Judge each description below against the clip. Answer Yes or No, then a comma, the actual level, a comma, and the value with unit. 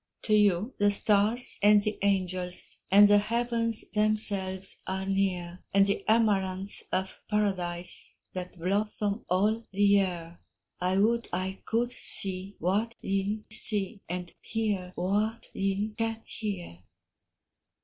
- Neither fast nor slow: No, slow, 125 wpm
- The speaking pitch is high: Yes, high, 200 Hz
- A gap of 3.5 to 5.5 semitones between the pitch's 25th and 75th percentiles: No, narrow, 2.4 semitones